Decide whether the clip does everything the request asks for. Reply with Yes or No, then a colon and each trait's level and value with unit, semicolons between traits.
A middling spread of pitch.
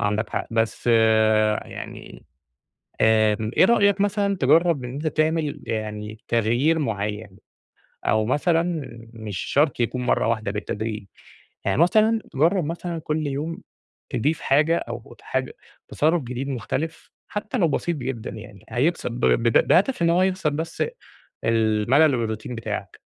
No: wide, 6.9 semitones